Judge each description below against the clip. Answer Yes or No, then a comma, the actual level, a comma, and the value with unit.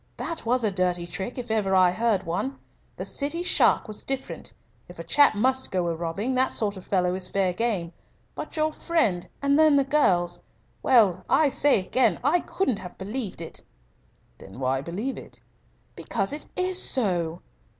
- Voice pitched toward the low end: No, high, 215 Hz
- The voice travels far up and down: Yes, wide, 6.9 semitones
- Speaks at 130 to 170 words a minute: No, average, 180 wpm